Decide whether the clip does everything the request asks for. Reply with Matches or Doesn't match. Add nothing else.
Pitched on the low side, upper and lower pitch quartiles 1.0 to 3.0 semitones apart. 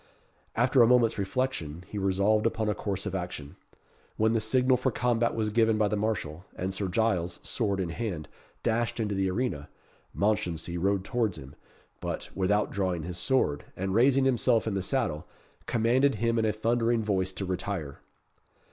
Doesn't match